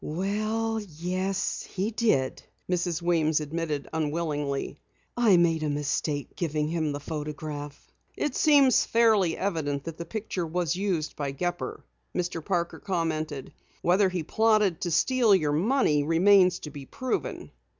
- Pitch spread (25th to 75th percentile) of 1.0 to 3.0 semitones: No, average, 4.5 semitones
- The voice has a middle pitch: Yes, medium, 170 Hz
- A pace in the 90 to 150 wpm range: Yes, average, 140 wpm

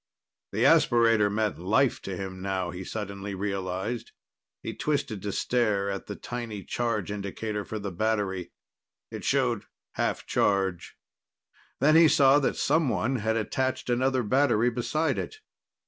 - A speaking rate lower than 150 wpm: Yes, average, 140 wpm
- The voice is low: Yes, low, 110 Hz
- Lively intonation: No, average, 3.9 semitones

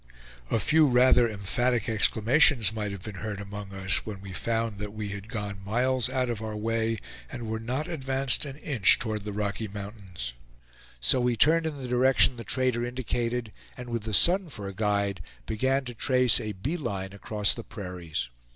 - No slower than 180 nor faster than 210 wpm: Yes, average, 190 wpm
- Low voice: Yes, low, 110 Hz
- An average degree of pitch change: Yes, average, 3.9 semitones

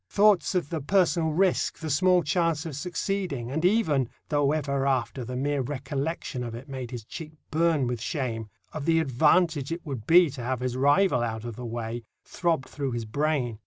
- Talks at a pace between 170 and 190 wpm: Yes, average, 185 wpm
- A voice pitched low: No, medium, 145 Hz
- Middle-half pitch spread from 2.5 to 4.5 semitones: No, average, 4.9 semitones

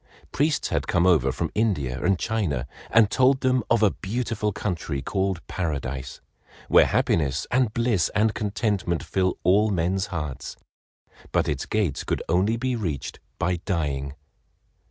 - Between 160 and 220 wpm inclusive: No, average, 145 wpm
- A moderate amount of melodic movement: No, wide, 5.8 semitones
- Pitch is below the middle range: Yes, very low, 95 Hz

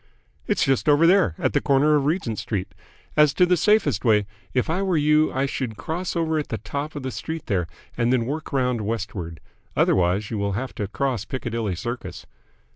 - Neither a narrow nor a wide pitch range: No, wide, 6.0 semitones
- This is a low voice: Yes, low, 130 Hz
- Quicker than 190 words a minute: Yes, average, 200 wpm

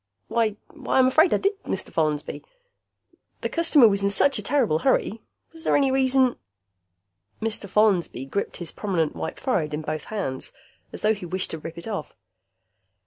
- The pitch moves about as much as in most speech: No, wide, 8.6 semitones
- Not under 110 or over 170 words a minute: No, average, 180 wpm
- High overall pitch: Yes, high, 200 Hz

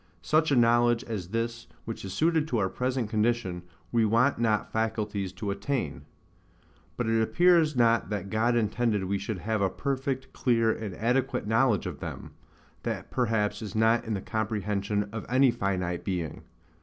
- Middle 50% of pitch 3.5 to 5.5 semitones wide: No, average, 2.8 semitones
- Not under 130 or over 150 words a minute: No, average, 170 wpm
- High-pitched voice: No, low, 110 Hz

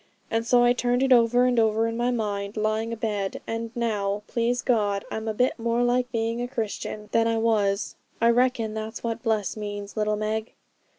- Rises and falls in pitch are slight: Yes, narrow, 2.1 semitones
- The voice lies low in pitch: No, high, 225 Hz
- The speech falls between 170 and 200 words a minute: Yes, average, 195 wpm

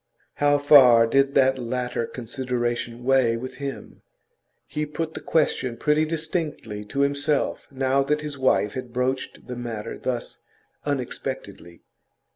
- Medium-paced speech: No, slow, 130 wpm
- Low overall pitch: Yes, low, 130 Hz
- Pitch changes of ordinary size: Yes, average, 3.1 semitones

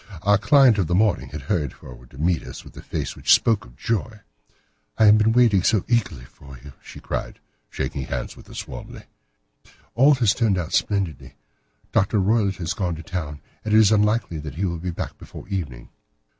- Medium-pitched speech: No, very low, 95 Hz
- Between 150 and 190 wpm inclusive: No, average, 200 wpm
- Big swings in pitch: Yes, wide, 6.2 semitones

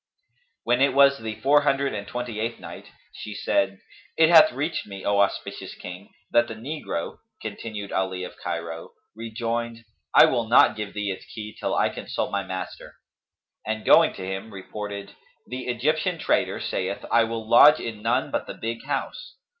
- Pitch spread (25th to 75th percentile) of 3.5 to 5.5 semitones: Yes, average, 3.9 semitones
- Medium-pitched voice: No, low, 115 Hz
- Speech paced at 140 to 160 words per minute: No, average, 175 wpm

